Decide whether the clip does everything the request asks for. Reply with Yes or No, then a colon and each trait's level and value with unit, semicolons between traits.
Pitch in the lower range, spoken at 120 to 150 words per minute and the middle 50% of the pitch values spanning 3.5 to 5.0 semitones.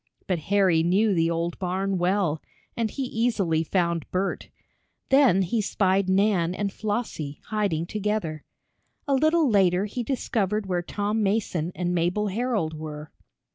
No: high, 195 Hz; average, 140 wpm; average, 3.9 semitones